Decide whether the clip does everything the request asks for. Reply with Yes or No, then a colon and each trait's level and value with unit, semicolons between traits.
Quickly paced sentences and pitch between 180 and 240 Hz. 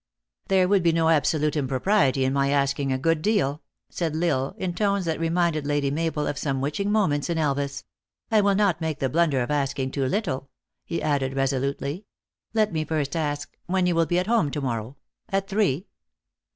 No: fast, 210 wpm; medium, 155 Hz